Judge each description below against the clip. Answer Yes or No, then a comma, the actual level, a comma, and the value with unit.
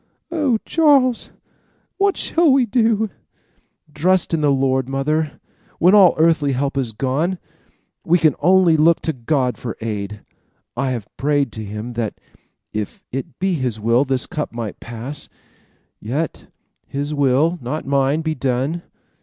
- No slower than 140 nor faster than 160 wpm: Yes, average, 145 wpm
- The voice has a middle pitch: Yes, medium, 145 Hz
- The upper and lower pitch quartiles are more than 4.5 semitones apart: Yes, average, 5.3 semitones